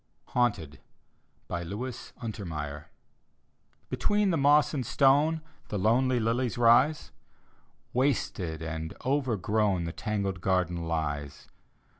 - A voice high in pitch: No, low, 110 Hz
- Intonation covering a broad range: Yes, wide, 7.4 semitones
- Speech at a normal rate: No, slow, 95 wpm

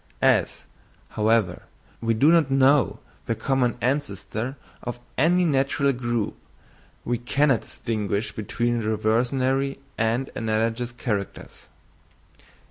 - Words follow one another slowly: Yes, slow, 100 wpm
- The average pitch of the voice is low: Yes, low, 120 Hz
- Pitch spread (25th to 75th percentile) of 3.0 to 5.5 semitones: Yes, average, 3.3 semitones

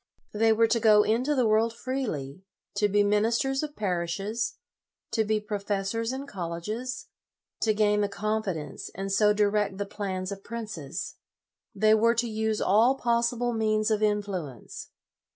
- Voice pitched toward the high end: Yes, high, 215 Hz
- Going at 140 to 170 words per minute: Yes, average, 150 wpm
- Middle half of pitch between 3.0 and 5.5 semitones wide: No, narrow, 2.4 semitones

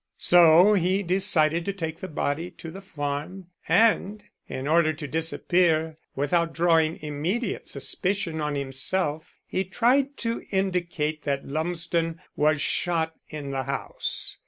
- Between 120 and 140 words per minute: Yes, slow, 135 wpm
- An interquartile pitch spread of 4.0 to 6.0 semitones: No, average, 3.4 semitones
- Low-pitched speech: No, medium, 165 Hz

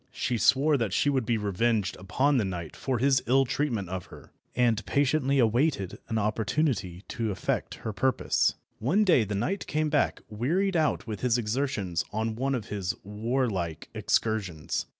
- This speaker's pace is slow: No, average, 170 wpm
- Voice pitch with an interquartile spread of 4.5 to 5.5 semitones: Yes, average, 4.9 semitones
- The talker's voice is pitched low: Yes, low, 115 Hz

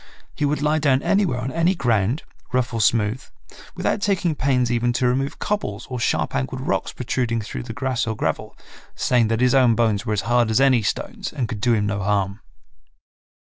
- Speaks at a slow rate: No, average, 200 wpm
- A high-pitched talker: No, low, 125 Hz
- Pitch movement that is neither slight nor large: Yes, average, 3.7 semitones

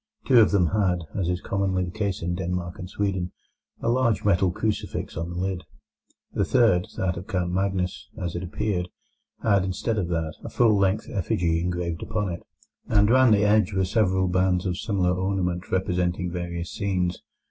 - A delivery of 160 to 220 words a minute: Yes, average, 180 wpm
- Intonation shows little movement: Yes, narrow, 2.3 semitones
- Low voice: Yes, very low, 95 Hz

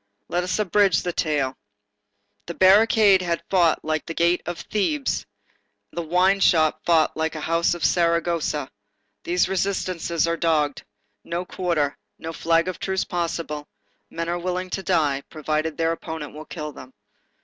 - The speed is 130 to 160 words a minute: Yes, average, 155 wpm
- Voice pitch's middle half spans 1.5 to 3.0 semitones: Yes, narrow, 2.5 semitones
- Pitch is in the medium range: Yes, medium, 170 Hz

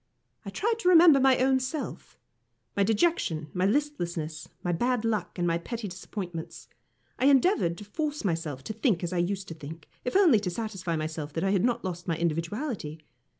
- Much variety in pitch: Yes, wide, 7.5 semitones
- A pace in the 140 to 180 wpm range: No, average, 190 wpm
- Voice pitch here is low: No, high, 195 Hz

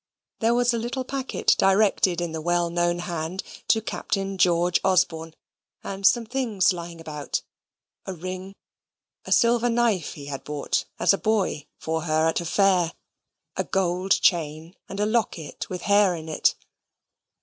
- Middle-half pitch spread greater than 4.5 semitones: No, average, 4.0 semitones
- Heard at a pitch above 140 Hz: Yes, medium, 185 Hz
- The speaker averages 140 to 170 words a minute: Yes, average, 160 wpm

